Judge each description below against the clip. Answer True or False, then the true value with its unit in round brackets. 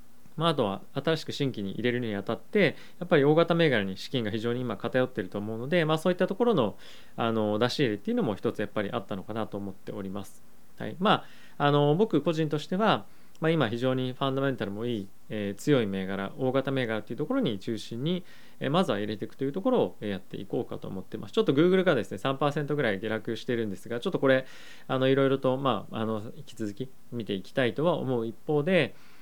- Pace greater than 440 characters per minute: True (460 characters per minute)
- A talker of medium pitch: False (125 Hz)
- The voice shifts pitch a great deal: True (5.7 semitones)